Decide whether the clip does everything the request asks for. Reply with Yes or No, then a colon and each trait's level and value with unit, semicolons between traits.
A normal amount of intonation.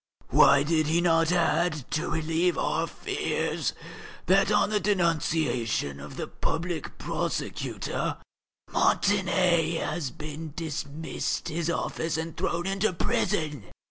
No: narrow, 2.3 semitones